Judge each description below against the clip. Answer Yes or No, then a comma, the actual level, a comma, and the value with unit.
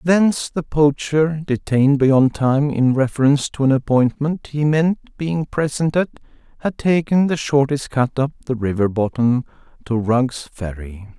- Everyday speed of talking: Yes, average, 150 wpm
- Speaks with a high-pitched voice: No, medium, 140 Hz